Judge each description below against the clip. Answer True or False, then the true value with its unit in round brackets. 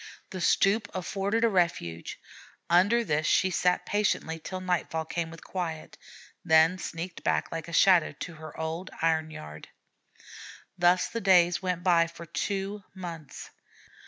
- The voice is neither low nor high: True (175 Hz)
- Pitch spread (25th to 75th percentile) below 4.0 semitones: True (2.6 semitones)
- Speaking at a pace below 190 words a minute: True (145 wpm)